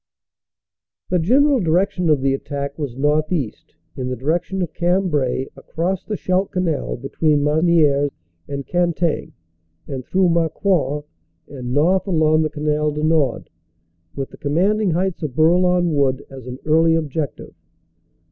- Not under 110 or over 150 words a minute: Yes, average, 140 wpm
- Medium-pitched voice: Yes, medium, 155 Hz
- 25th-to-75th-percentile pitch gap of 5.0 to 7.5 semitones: No, average, 3.9 semitones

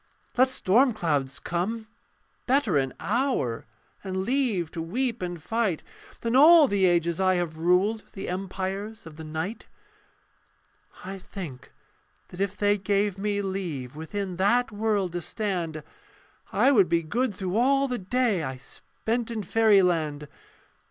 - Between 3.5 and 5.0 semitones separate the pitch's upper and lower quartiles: Yes, average, 4.6 semitones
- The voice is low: No, high, 195 Hz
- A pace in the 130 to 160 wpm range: Yes, average, 145 wpm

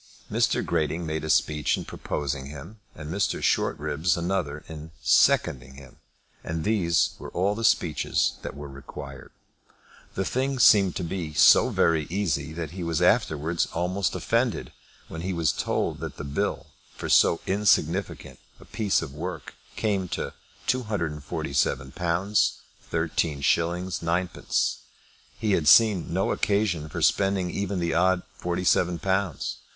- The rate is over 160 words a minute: No, average, 140 wpm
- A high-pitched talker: No, very low, 85 Hz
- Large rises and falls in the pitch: No, average, 3.9 semitones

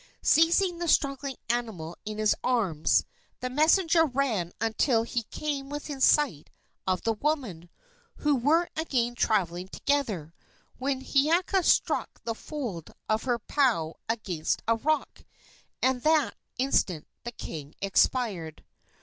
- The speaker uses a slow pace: Yes, slow, 125 wpm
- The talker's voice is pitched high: Yes, high, 245 Hz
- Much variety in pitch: Yes, wide, 6.3 semitones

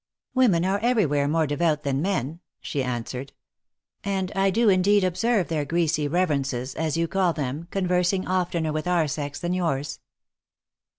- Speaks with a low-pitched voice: No, medium, 170 Hz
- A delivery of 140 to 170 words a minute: Yes, average, 165 wpm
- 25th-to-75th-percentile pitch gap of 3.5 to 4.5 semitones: Yes, average, 4.2 semitones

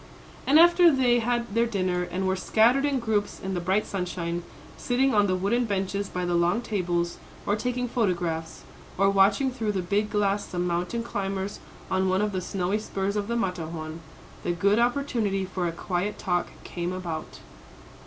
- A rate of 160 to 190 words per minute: Yes, average, 180 wpm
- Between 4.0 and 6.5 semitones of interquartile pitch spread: Yes, average, 4.4 semitones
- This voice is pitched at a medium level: No, high, 195 Hz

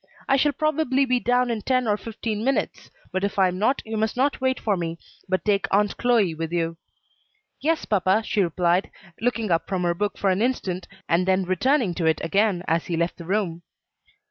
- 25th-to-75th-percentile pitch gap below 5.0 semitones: No, wide, 5.5 semitones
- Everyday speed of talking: No, fast, 210 wpm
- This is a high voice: Yes, high, 205 Hz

